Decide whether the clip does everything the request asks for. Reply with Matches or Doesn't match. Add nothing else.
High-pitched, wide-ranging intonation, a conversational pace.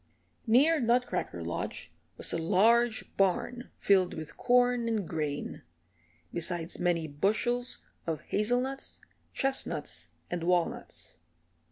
Doesn't match